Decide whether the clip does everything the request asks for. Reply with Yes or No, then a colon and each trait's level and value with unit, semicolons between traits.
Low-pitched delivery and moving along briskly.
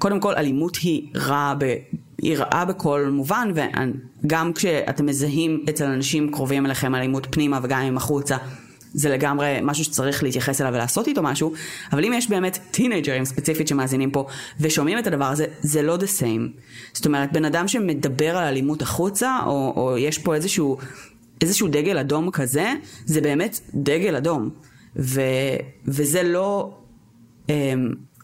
No: medium, 145 Hz; fast, 155 wpm